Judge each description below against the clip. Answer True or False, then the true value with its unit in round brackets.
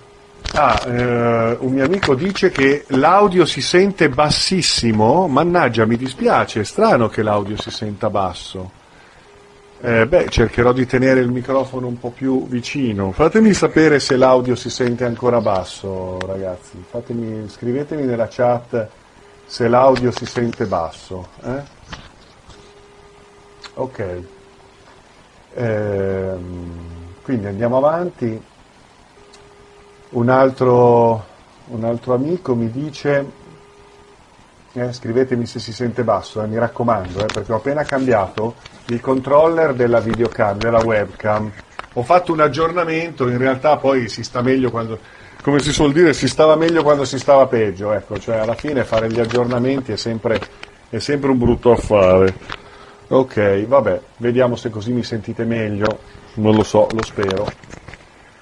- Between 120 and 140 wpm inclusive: True (135 wpm)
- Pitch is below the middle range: True (120 Hz)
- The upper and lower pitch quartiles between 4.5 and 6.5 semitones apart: False (3.6 semitones)